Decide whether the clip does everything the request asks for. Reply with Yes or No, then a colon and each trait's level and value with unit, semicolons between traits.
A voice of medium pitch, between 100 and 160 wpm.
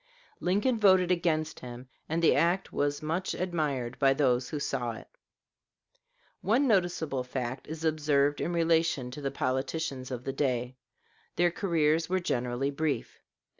Yes: medium, 150 Hz; average, 145 wpm